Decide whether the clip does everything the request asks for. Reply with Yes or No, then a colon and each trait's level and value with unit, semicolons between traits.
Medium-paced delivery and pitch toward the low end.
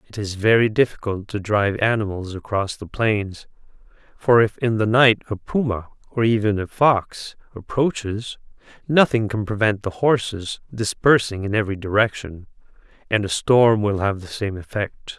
Yes: average, 155 wpm; low, 105 Hz